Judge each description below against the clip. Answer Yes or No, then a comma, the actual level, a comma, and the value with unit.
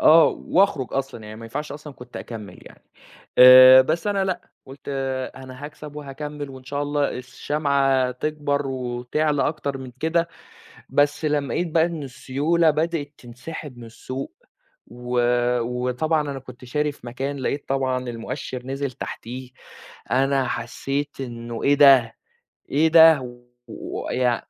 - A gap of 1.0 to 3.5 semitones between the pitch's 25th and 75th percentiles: Yes, average, 2.8 semitones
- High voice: No, low, 135 Hz